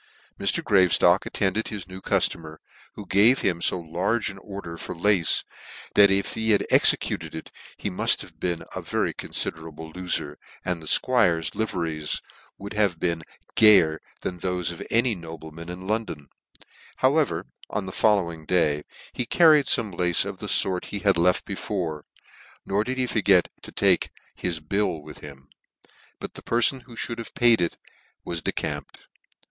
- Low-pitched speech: Yes, very low, 90 Hz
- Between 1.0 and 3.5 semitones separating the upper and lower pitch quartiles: No, average, 4.2 semitones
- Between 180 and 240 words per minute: No, average, 165 wpm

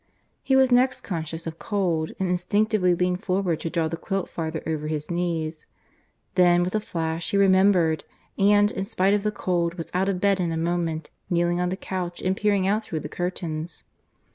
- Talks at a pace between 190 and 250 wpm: Yes, average, 195 wpm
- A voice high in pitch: No, medium, 180 Hz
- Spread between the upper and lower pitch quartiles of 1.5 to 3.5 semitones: Yes, average, 3.0 semitones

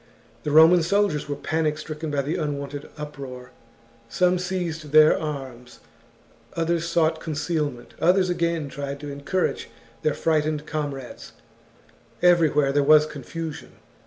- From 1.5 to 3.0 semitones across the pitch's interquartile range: Yes, narrow, 2.6 semitones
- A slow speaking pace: Yes, slow, 130 wpm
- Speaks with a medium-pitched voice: Yes, medium, 155 Hz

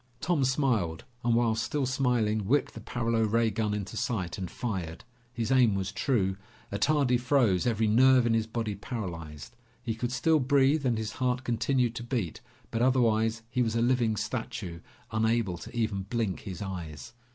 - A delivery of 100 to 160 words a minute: No, average, 175 wpm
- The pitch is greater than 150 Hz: No, low, 115 Hz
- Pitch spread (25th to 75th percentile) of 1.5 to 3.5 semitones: Yes, average, 3.1 semitones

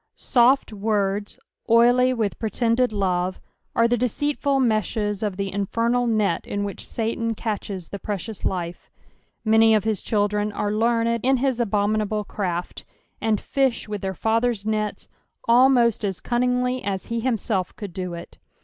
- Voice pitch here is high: Yes, high, 220 Hz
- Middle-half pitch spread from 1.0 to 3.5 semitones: Yes, average, 2.8 semitones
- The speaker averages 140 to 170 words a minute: Yes, average, 150 wpm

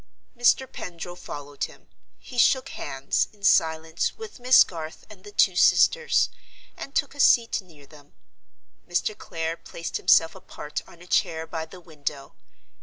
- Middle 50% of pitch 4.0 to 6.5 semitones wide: Yes, average, 4.9 semitones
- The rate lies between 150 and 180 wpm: Yes, average, 155 wpm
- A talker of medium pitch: Yes, medium, 170 Hz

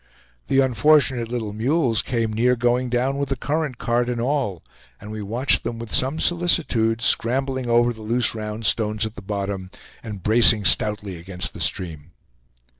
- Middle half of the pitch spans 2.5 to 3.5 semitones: Yes, average, 3.2 semitones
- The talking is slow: No, average, 170 wpm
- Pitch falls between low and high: No, low, 115 Hz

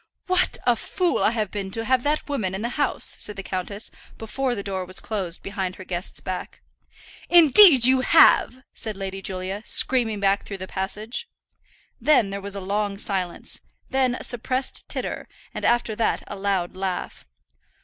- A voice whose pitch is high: Yes, high, 210 Hz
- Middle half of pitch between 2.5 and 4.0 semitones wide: No, average, 4.6 semitones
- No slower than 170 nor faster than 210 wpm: Yes, average, 175 wpm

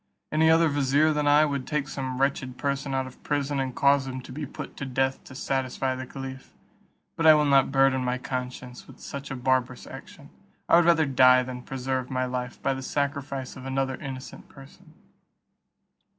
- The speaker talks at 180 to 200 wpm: Yes, average, 195 wpm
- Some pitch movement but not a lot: No, narrow, 1.6 semitones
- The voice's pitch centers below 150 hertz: Yes, low, 135 Hz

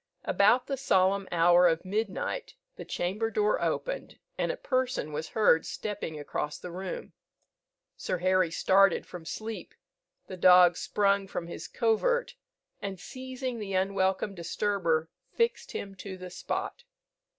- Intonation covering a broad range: No, average, 3.7 semitones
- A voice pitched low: No, high, 195 Hz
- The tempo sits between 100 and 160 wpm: Yes, average, 140 wpm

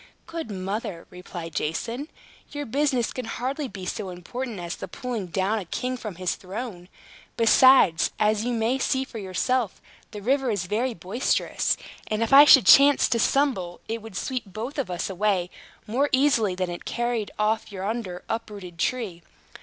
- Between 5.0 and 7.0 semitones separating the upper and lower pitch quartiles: Yes, average, 5.3 semitones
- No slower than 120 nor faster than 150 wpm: No, average, 170 wpm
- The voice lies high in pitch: Yes, high, 220 Hz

